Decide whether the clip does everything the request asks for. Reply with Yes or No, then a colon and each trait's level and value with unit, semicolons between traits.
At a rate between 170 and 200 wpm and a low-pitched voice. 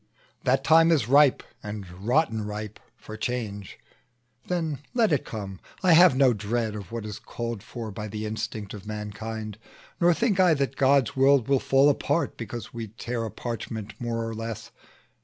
Yes: average, 175 wpm; low, 115 Hz